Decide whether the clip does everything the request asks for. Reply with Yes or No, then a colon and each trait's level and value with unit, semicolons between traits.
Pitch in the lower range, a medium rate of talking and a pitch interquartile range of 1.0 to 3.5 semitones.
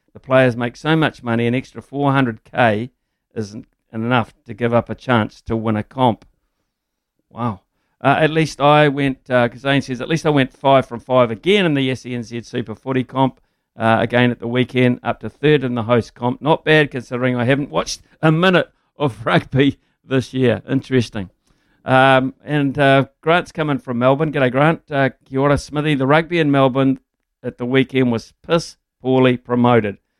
Yes: low, 130 Hz; average, 180 wpm; average, 2.9 semitones